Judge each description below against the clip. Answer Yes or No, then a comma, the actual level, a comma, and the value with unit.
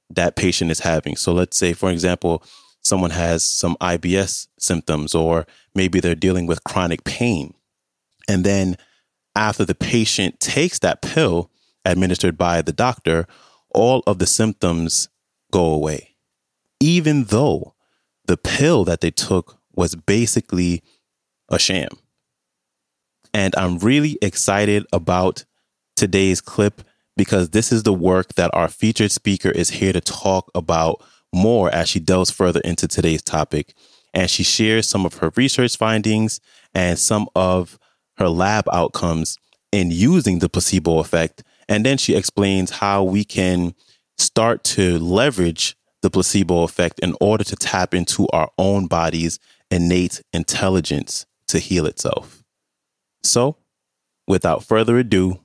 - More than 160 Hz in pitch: No, very low, 90 Hz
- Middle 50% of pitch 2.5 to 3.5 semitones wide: Yes, average, 3.2 semitones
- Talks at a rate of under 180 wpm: Yes, average, 140 wpm